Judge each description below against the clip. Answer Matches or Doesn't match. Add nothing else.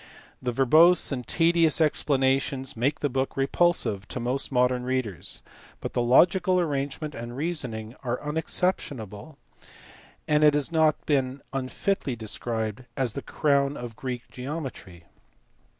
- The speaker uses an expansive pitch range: Doesn't match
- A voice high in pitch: Doesn't match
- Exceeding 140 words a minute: Doesn't match